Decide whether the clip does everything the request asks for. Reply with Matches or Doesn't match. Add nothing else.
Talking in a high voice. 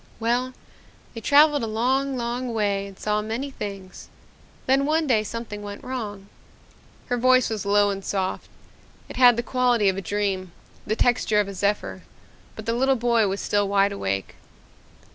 Matches